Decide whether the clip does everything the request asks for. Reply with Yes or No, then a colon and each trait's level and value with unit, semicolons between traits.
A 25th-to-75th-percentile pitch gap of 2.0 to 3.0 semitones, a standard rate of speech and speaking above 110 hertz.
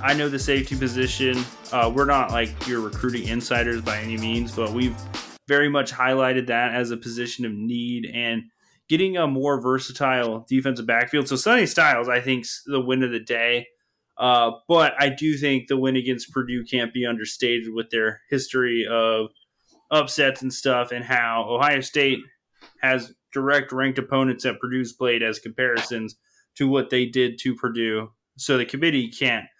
Yes: narrow, 2.4 semitones; average, 170 wpm; low, 125 Hz